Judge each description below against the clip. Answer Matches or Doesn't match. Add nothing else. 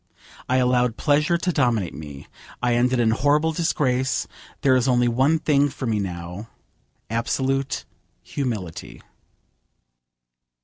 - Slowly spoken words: Matches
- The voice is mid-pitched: Doesn't match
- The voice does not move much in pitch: Doesn't match